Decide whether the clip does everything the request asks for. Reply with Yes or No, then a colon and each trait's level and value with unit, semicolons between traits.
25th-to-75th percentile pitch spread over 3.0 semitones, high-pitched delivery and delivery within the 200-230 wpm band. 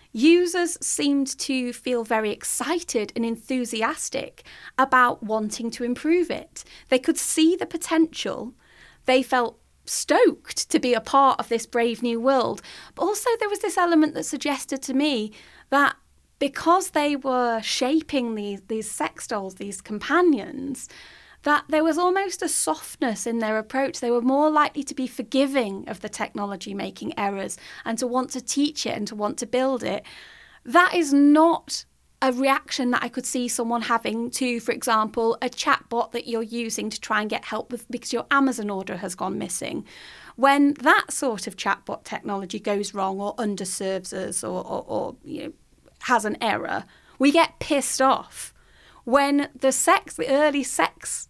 No: average, 4.1 semitones; very high, 255 Hz; average, 170 wpm